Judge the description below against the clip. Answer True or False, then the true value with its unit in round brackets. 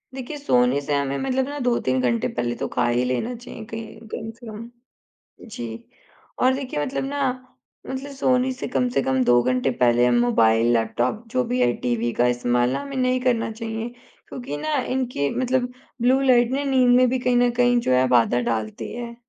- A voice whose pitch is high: True (225 Hz)